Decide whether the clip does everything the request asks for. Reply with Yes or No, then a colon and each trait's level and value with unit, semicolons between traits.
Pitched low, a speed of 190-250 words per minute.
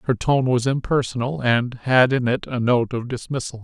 Yes: low, 125 Hz; average, 200 wpm